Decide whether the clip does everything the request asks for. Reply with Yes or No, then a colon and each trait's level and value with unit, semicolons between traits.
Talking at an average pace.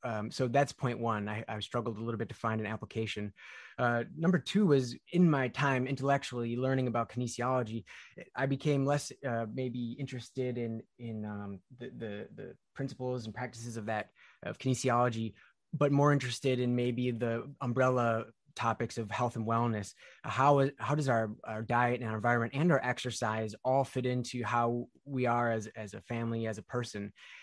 Yes: average, 180 wpm